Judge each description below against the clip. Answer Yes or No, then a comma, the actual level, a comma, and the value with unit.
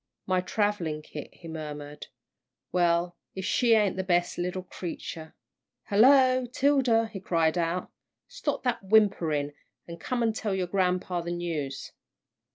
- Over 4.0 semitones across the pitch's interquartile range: Yes, average, 4.5 semitones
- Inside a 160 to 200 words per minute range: No, slow, 135 wpm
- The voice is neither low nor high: Yes, medium, 180 Hz